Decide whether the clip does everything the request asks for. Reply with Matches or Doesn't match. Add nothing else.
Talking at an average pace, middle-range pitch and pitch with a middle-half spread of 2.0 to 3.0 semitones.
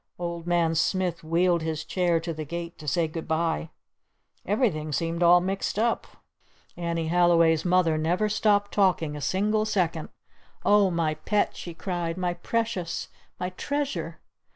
Matches